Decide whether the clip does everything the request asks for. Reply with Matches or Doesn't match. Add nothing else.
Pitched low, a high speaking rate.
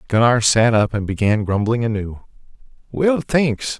Doesn't match